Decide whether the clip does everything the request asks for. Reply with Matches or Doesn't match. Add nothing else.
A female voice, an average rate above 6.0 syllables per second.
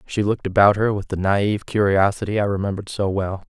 Doesn't match